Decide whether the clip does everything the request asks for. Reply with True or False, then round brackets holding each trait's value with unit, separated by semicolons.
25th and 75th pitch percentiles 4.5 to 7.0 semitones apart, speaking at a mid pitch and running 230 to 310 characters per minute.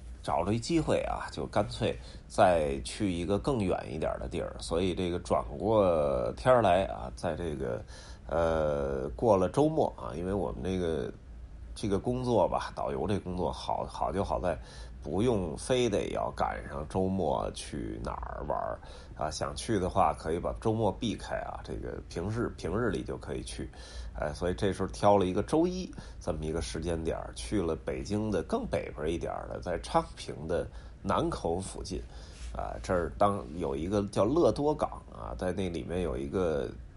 False (5.4 semitones; 90 Hz; 255 characters per minute)